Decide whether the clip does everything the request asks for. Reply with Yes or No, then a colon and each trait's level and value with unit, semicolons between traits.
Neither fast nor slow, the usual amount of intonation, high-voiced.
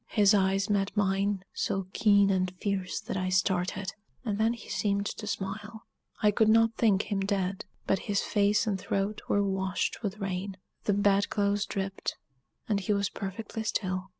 No: average, 175 wpm; narrow, 1.3 semitones; high, 200 Hz